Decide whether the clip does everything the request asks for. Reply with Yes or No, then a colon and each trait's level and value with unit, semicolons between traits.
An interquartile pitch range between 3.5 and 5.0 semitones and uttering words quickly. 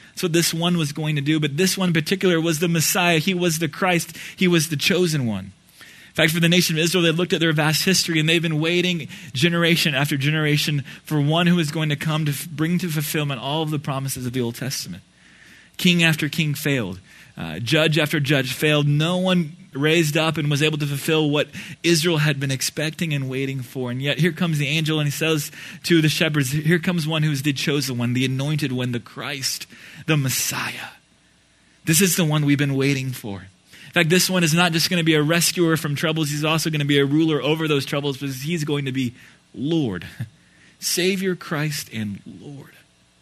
No: average, 3.0 semitones; fast, 220 wpm